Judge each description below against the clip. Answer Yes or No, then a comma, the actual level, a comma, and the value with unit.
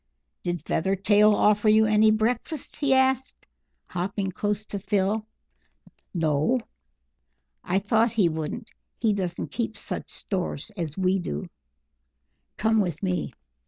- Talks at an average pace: No, slow, 125 wpm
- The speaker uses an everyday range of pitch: Yes, average, 3.2 semitones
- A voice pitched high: Yes, high, 205 Hz